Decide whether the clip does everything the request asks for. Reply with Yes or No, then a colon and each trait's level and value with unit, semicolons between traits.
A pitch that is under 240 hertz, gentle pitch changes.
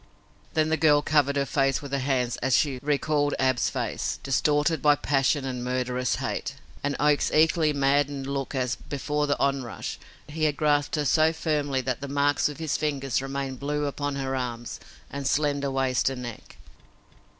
Yes: medium, 140 Hz; narrow, 1.8 semitones